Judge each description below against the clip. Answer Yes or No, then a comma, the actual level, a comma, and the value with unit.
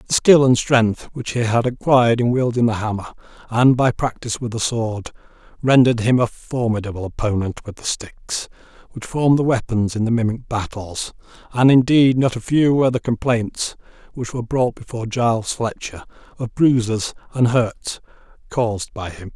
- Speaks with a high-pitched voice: No, low, 120 Hz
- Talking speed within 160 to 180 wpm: Yes, average, 170 wpm